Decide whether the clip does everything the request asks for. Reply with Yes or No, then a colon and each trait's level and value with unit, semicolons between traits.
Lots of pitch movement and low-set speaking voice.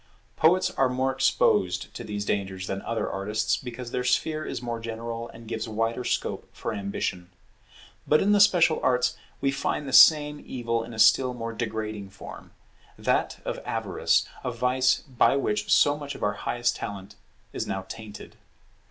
No: average, 3.6 semitones; low, 115 Hz